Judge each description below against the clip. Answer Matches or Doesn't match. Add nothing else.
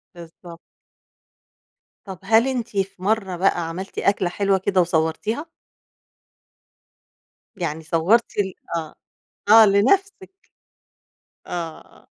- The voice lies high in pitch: Matches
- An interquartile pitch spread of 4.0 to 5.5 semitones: Matches